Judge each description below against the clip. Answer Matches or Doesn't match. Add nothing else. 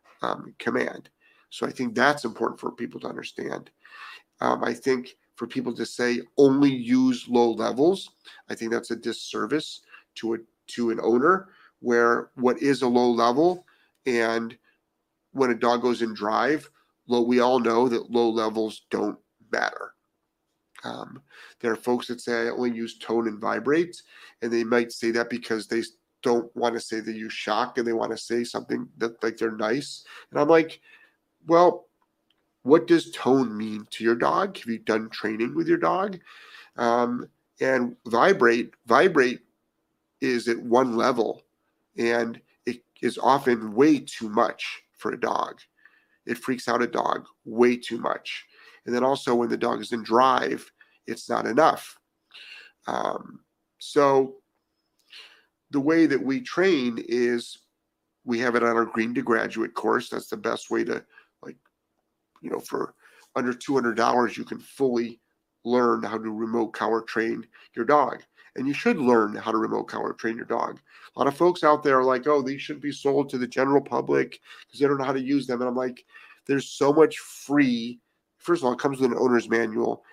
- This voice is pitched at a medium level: Doesn't match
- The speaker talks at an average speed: Matches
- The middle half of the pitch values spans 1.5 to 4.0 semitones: Matches